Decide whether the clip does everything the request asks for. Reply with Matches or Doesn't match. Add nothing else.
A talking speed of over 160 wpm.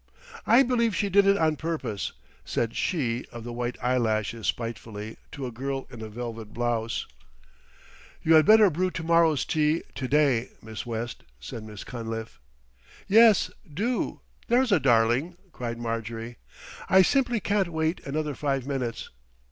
Doesn't match